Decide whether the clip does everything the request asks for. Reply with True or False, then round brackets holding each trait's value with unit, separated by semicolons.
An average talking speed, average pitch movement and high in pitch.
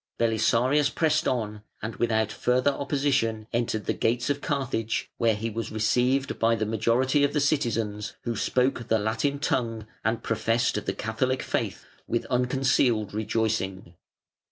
False (145 wpm; 3.1 semitones; 115 Hz)